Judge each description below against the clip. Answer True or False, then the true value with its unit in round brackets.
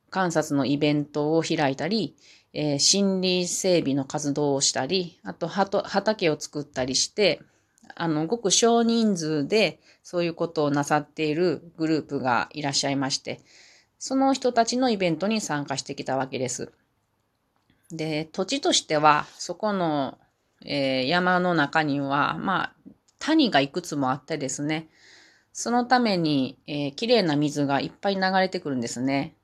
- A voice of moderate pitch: True (155 Hz)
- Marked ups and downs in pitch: False (4.9 semitones)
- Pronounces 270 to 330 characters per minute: True (295 characters per minute)